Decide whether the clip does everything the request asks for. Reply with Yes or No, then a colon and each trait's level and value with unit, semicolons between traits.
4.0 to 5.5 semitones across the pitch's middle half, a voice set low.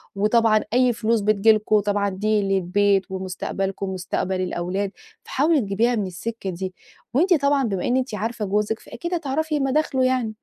No: average, 4.5 semitones; high, 215 Hz